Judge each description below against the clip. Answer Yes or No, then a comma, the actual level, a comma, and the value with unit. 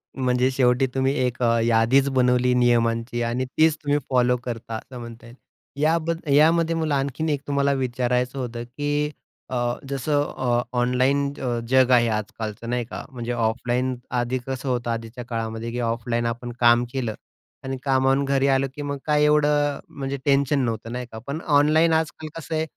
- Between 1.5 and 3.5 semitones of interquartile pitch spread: Yes, average, 2.9 semitones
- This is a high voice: No, low, 130 Hz